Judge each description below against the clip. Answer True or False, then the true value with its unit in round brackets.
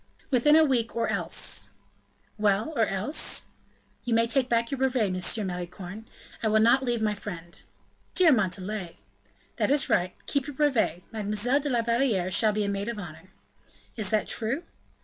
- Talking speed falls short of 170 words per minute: False (175 wpm)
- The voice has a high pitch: True (220 Hz)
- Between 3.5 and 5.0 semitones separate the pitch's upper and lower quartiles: True (4.3 semitones)